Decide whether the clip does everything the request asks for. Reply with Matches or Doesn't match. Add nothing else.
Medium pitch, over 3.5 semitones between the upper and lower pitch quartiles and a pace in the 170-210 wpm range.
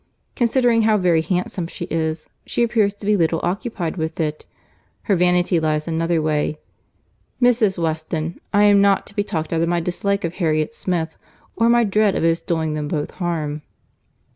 Matches